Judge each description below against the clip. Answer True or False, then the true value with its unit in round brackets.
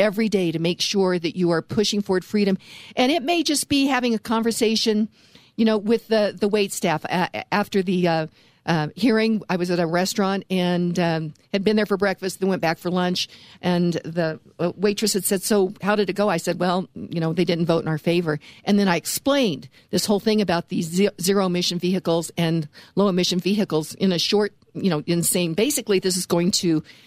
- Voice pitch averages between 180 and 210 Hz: True (185 Hz)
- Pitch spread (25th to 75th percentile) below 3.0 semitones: False (3.3 semitones)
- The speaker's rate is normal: False (215 wpm)